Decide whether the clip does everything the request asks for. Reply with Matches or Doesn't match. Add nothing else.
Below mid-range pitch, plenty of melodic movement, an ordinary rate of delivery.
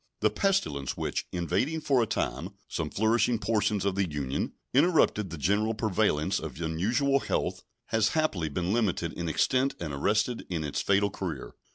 Matches